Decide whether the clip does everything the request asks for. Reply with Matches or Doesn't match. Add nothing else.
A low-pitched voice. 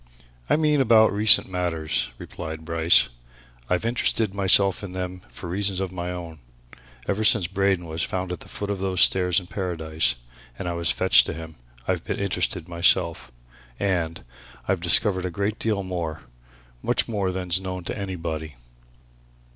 Matches